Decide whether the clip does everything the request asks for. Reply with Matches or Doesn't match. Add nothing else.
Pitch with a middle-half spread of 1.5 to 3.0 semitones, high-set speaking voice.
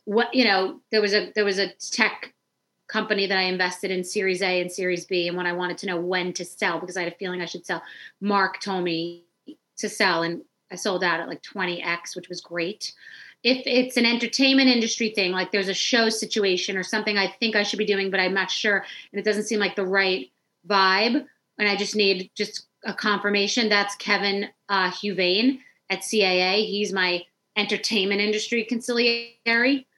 Matches